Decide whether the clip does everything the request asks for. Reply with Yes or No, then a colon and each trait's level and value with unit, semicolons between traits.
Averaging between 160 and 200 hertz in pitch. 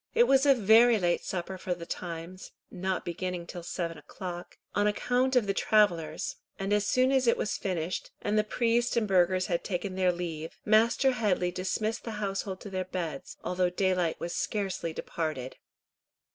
Yes: high, 190 Hz